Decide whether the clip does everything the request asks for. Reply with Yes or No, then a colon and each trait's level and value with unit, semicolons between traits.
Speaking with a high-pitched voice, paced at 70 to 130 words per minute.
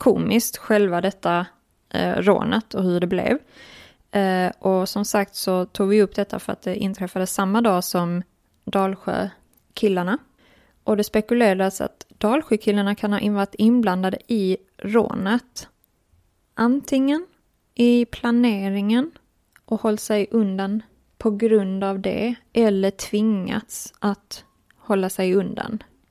Yes: high, 205 Hz; slow, 125 wpm